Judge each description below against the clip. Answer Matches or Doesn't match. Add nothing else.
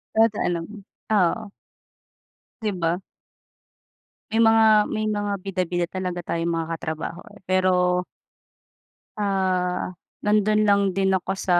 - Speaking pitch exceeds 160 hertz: Matches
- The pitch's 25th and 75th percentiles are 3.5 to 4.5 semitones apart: Doesn't match